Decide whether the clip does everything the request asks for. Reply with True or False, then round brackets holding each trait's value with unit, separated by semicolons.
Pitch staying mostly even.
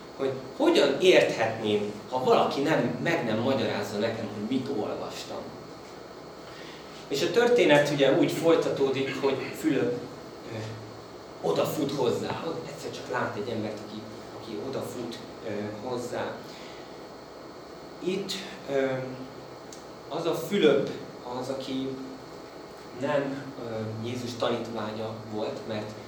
False (3.7 semitones)